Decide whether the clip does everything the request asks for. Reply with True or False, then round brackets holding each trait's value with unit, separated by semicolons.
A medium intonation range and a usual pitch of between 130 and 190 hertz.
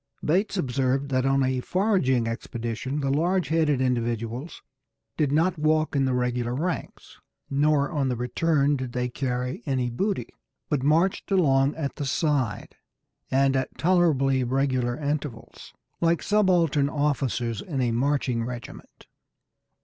True (3.7 semitones; 135 Hz)